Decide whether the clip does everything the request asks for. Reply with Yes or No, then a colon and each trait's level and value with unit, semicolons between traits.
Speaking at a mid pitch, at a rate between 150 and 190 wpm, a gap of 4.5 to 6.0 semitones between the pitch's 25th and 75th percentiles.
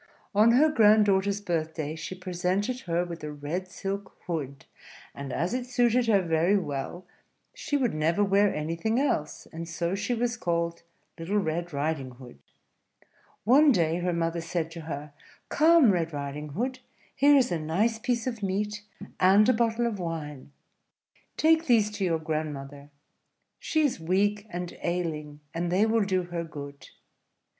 Yes: medium, 180 Hz; average, 160 wpm; wide, 5.4 semitones